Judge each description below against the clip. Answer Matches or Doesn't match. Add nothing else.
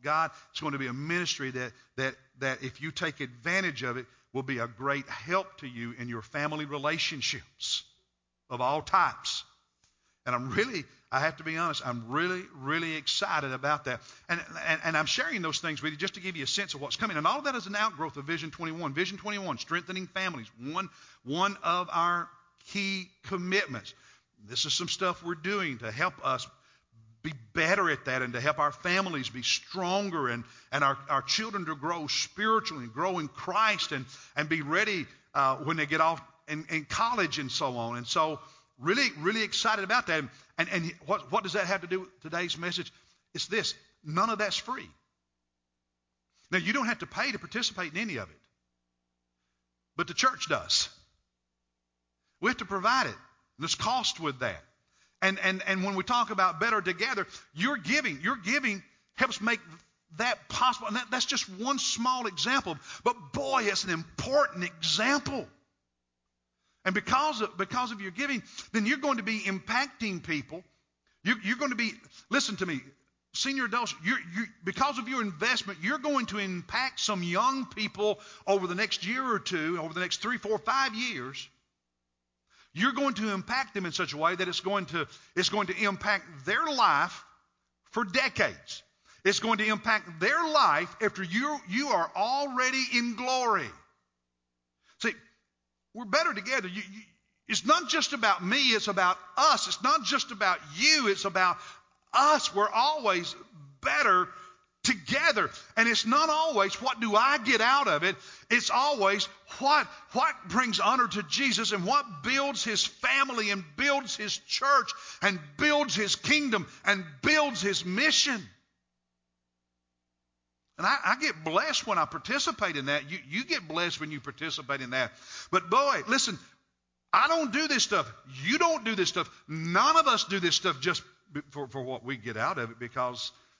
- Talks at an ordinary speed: Matches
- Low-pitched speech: Doesn't match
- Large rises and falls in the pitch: Matches